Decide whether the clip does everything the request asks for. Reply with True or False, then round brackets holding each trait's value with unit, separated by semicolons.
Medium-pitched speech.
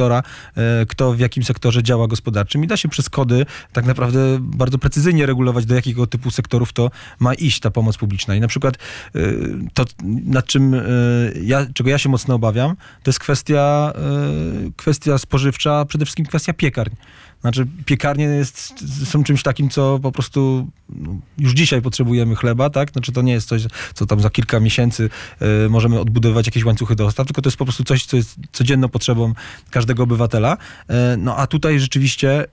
False (125 Hz)